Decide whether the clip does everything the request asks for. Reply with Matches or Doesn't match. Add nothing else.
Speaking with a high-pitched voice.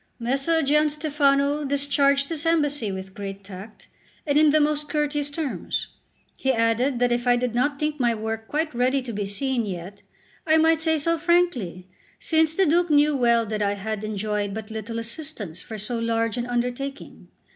Matches